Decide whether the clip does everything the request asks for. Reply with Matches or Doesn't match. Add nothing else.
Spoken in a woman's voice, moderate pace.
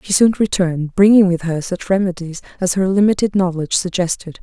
Matches